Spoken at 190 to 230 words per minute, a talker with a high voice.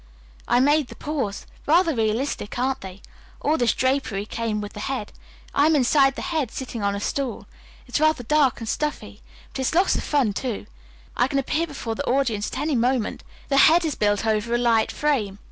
Yes: average, 200 wpm; very high, 255 Hz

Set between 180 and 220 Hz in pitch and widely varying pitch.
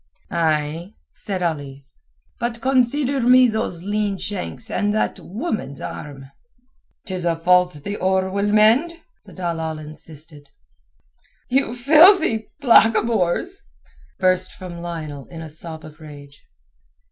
Yes: medium, 185 Hz; wide, 6.1 semitones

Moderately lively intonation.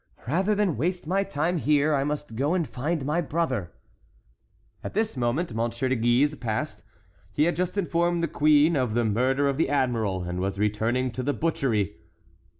No: wide, 5.9 semitones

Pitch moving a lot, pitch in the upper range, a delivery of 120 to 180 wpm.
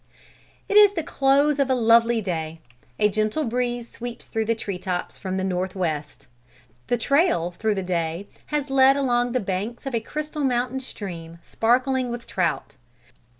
Yes: wide, 5.9 semitones; high, 230 Hz; average, 170 wpm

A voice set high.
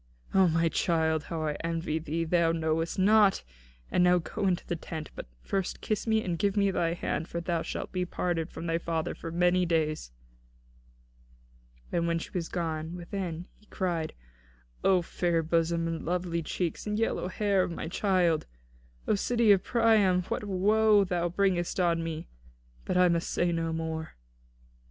No: medium, 175 Hz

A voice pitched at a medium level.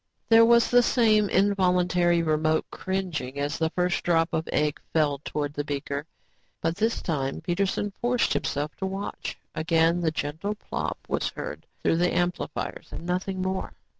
Yes: medium, 175 Hz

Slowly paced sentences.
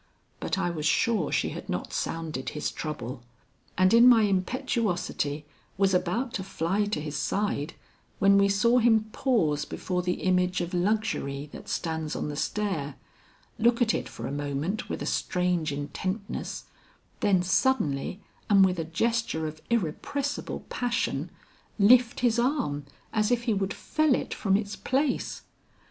No: average, 155 wpm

